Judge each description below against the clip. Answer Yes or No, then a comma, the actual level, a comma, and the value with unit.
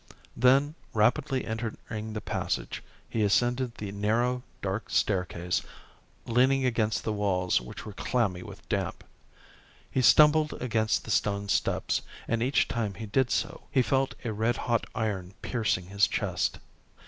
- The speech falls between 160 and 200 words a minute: No, average, 145 wpm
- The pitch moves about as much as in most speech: Yes, average, 3.5 semitones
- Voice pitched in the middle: No, low, 110 Hz